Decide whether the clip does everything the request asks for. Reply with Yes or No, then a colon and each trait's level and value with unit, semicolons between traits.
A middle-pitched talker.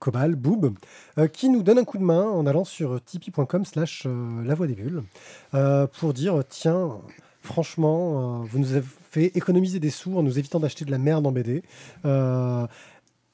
Yes: medium, 155 Hz